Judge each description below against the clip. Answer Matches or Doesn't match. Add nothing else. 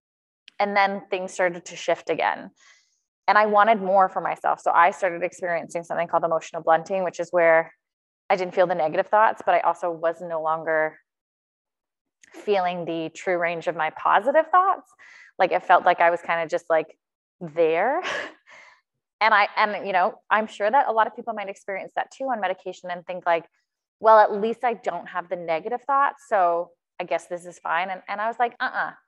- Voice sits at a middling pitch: Matches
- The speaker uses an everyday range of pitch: Matches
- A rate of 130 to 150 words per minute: Doesn't match